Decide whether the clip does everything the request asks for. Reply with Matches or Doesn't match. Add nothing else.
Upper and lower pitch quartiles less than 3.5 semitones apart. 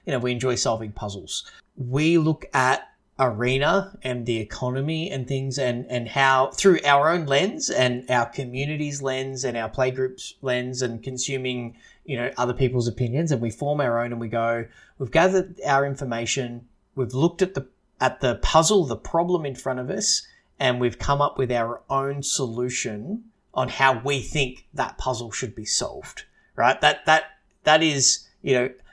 Matches